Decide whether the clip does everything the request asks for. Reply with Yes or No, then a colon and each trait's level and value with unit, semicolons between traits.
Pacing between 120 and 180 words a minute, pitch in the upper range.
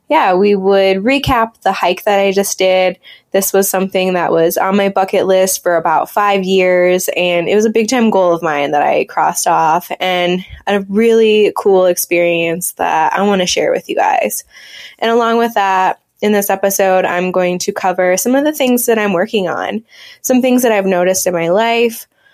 No: fast, 205 wpm; high, 195 Hz